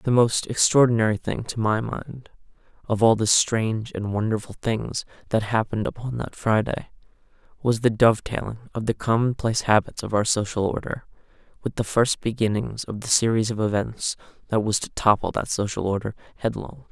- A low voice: Yes, low, 110 Hz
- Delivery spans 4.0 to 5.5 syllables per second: Yes, 5.4 syllables/s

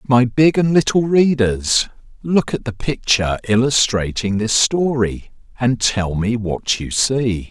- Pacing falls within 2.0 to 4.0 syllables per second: Yes, 3.9 syllables/s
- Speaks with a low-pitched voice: Yes, low, 120 Hz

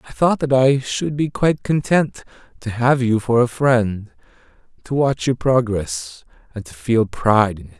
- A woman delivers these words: No, male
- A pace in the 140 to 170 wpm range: No, average, 185 wpm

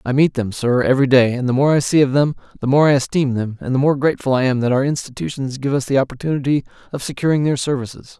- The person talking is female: No, male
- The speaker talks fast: Yes, fast, 255 wpm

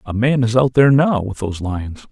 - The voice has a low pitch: Yes, low, 115 Hz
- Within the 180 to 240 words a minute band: No, fast, 255 wpm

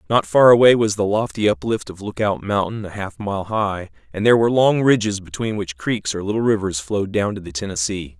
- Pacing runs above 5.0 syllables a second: Yes, 5.7 syllables/s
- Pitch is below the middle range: Yes, low, 100 Hz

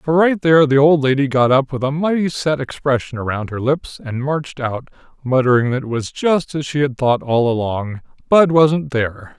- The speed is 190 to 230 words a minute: Yes, fast, 205 wpm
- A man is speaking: Yes, male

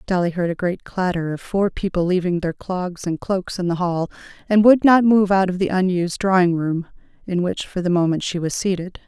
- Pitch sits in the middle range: Yes, medium, 180 Hz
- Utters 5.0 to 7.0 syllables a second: Yes, 5.3 syllables/s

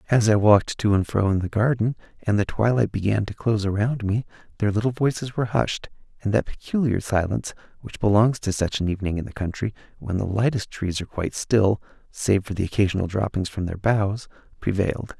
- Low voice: Yes, low, 105 Hz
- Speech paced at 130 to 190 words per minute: No, average, 200 wpm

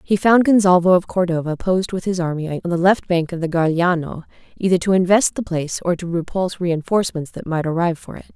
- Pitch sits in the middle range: Yes, medium, 175 Hz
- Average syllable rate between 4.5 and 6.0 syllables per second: No, 6.4 syllables/s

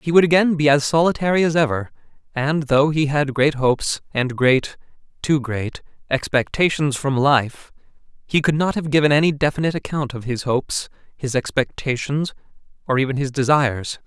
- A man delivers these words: Yes, male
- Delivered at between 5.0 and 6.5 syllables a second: Yes, 5.3 syllables/s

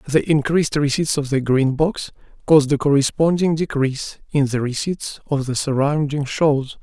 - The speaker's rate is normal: Yes, average, 160 wpm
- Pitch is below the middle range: No, medium, 145 Hz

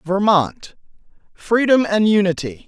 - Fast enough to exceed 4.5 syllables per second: No, 4.0 syllables/s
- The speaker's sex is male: Yes, male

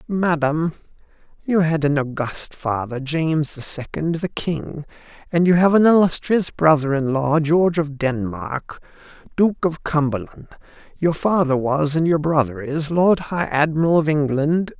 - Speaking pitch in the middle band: Yes, medium, 155 Hz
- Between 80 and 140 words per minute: No, average, 150 wpm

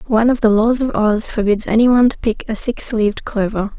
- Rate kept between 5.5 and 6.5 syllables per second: Yes, 5.7 syllables/s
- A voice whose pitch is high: Yes, high, 220 Hz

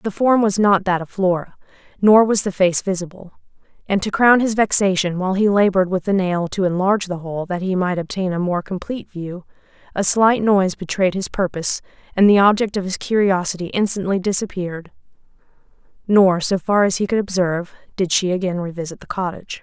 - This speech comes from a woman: Yes, female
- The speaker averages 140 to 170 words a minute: No, average, 190 wpm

